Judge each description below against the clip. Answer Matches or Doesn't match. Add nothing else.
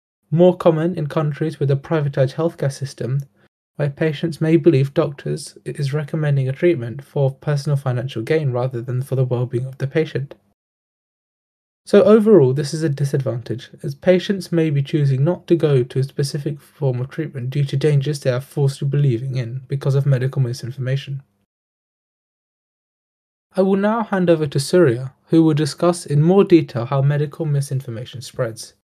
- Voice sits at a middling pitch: Matches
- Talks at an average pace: Matches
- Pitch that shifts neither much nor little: Matches